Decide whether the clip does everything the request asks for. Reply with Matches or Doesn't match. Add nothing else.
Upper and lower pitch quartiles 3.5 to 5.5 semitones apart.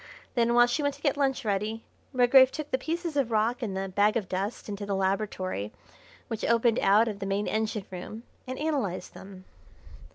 Matches